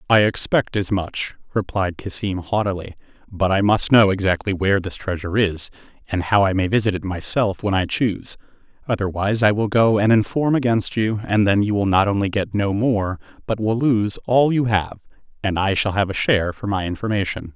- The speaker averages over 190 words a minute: Yes, average, 200 wpm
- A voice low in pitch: Yes, low, 100 Hz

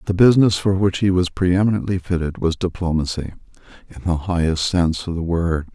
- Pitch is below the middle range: Yes, very low, 90 Hz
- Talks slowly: No, average, 175 wpm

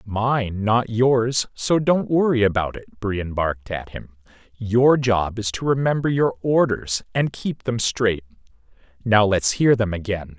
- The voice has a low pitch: Yes, low, 110 Hz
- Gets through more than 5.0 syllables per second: No, 4.0 syllables/s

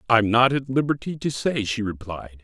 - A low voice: Yes, low, 115 Hz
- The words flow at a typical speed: Yes, average, 195 wpm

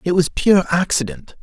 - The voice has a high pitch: No, medium, 165 Hz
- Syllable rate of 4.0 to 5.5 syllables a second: Yes, 4.9 syllables/s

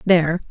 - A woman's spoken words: Yes, female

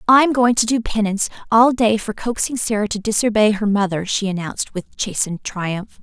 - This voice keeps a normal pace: Yes, average, 190 wpm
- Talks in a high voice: Yes, high, 215 Hz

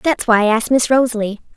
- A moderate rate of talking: No, fast, 230 wpm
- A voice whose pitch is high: Yes, high, 235 Hz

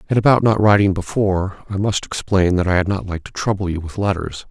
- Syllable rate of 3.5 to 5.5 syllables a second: No, 6.1 syllables/s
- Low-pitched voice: Yes, very low, 95 Hz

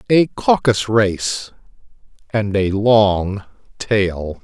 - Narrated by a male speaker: Yes, male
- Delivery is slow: Yes, slow, 95 wpm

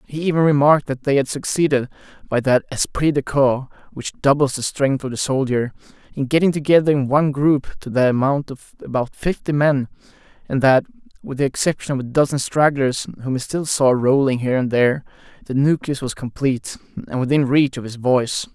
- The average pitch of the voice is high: No, low, 135 Hz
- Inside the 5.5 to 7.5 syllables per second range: Yes, 5.6 syllables/s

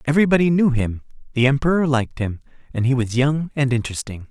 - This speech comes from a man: Yes, male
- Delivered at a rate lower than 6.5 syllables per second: No, 6.6 syllables/s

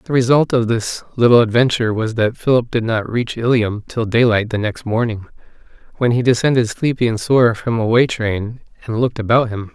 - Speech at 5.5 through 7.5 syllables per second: No, 5.3 syllables/s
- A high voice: No, low, 115 Hz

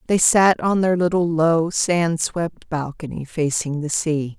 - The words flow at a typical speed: Yes, average, 165 wpm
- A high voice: No, medium, 165 Hz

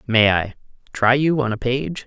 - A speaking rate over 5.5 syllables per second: No, 4.5 syllables/s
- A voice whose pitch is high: No, low, 125 Hz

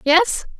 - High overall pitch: Yes, very high, 355 Hz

